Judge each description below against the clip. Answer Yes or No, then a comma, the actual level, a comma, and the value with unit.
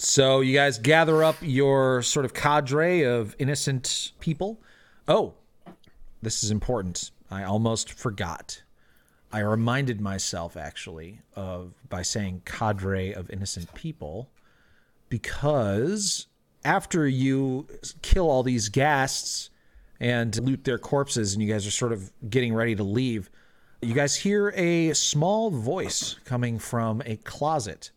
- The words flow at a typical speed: No, slow, 130 wpm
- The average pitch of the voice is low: Yes, low, 120 Hz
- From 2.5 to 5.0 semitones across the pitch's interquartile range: No, wide, 5.4 semitones